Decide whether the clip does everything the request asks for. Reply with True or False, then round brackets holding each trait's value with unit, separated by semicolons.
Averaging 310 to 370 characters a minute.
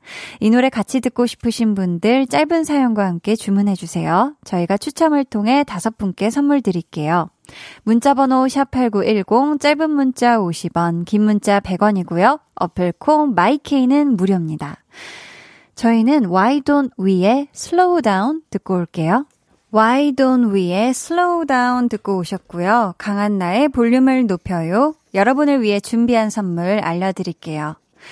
True (320 characters per minute)